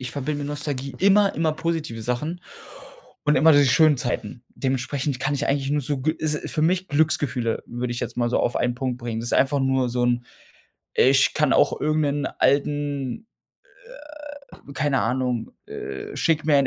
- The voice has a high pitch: No, medium, 140 Hz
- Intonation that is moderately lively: Yes, average, 3.3 semitones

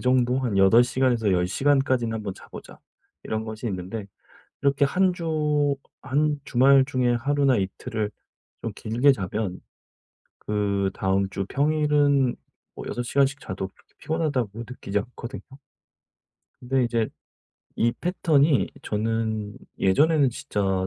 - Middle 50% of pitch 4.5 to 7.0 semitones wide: Yes, average, 5.3 semitones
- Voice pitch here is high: No, low, 120 Hz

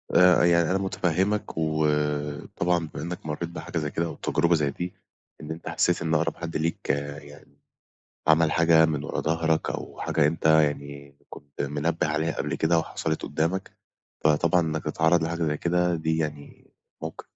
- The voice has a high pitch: No, very low, 80 Hz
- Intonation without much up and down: Yes, narrow, 2.1 semitones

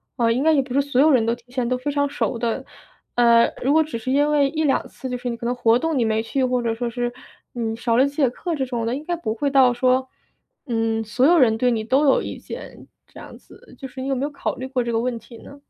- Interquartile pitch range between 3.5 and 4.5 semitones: No, average, 3.0 semitones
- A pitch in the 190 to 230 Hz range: No, very high, 250 Hz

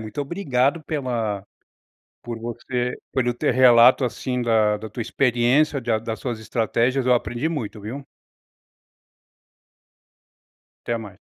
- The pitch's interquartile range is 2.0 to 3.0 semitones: Yes, narrow, 2.5 semitones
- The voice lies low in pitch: Yes, low, 120 Hz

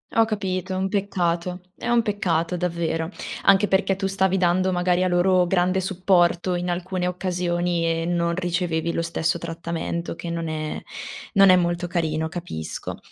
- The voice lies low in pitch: No, medium, 175 Hz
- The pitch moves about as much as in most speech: No, narrow, 1.8 semitones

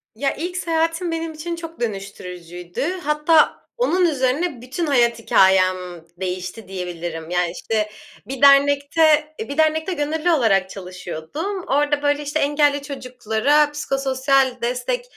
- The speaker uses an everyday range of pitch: No, wide, 8.1 semitones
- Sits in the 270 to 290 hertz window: Yes, very high, 280 Hz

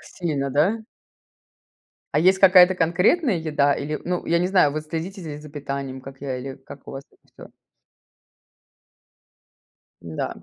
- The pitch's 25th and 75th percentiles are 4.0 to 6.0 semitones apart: Yes, average, 4.5 semitones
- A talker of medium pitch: Yes, medium, 155 Hz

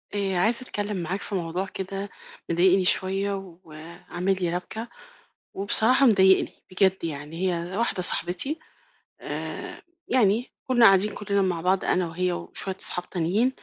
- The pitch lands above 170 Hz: Yes, high, 190 Hz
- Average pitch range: No, narrow, 2.3 semitones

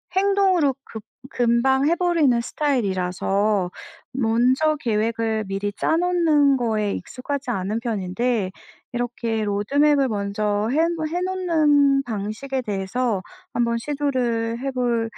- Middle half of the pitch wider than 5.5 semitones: No, average, 5.2 semitones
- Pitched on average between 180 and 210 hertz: No, high, 245 Hz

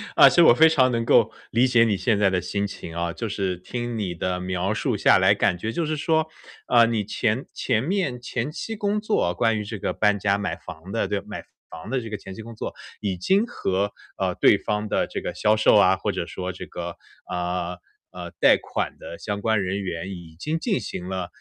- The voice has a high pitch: No, low, 105 Hz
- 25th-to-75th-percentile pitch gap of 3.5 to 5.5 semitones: Yes, average, 4.6 semitones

